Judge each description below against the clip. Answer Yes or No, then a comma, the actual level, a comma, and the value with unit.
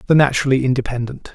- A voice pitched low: Yes, low, 130 Hz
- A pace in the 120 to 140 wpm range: Yes, slow, 135 wpm